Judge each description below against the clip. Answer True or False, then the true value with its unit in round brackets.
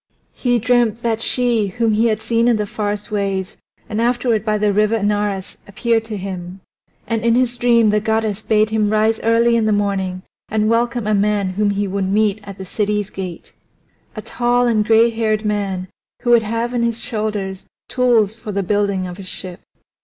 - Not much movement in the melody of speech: True (2.3 semitones)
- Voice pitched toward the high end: True (215 Hz)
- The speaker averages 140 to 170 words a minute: False (195 wpm)